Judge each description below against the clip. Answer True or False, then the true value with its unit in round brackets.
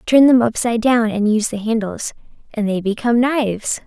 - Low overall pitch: False (225 Hz)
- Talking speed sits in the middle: True (185 wpm)